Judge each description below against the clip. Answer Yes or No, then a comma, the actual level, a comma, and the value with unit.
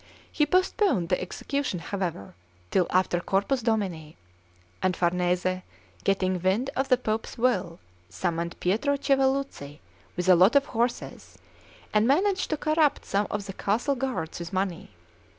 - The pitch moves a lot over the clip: Yes, wide, 7.0 semitones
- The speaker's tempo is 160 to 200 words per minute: No, average, 140 wpm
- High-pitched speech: Yes, high, 200 Hz